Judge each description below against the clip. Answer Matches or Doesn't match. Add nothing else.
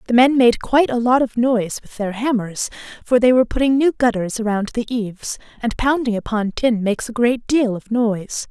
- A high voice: Matches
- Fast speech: Matches